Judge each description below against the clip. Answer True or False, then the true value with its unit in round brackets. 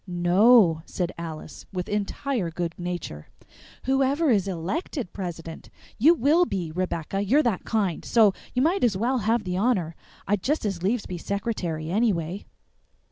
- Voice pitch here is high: True (195 Hz)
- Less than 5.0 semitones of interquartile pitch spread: False (5.6 semitones)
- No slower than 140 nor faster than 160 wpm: True (150 wpm)